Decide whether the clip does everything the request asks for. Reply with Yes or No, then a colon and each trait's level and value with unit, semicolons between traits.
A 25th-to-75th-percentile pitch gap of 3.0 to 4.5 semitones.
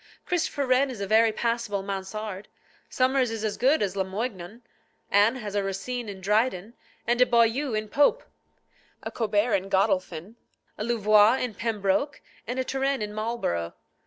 Yes: average, 3.7 semitones